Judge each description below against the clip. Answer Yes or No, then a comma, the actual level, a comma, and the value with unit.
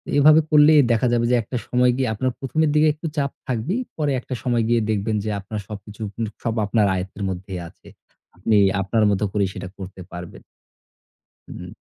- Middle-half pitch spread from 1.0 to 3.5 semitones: No, wide, 5.4 semitones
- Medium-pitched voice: No, low, 115 Hz